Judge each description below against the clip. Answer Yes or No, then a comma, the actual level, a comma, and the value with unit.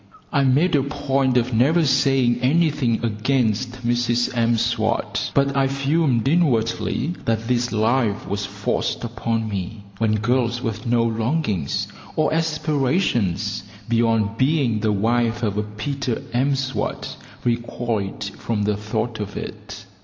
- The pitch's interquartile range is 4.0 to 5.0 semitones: No, average, 3.6 semitones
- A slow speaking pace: Yes, slow, 130 wpm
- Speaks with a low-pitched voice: Yes, low, 120 Hz